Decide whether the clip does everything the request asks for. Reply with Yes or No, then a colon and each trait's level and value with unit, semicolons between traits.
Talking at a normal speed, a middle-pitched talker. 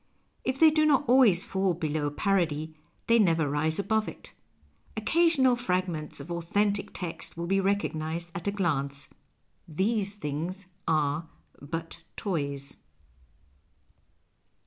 No: slow, 125 wpm; medium, 175 Hz